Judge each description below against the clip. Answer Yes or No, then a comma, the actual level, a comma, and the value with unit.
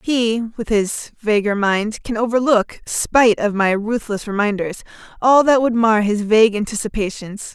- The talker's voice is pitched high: Yes, high, 220 Hz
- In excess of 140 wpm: No, slow, 135 wpm